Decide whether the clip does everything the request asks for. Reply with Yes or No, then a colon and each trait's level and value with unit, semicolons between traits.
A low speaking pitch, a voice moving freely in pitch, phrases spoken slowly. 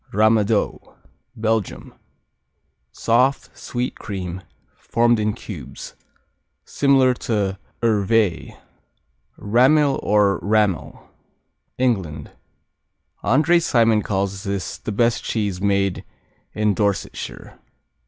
No: low, 105 Hz; average, 3.1 semitones; slow, 85 wpm